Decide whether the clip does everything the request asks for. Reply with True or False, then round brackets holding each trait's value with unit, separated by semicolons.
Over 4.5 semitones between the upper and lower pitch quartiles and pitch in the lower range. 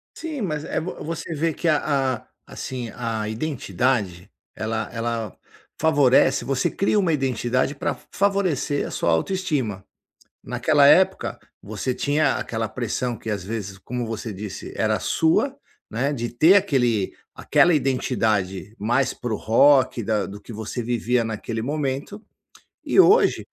True (5.1 semitones; 125 Hz)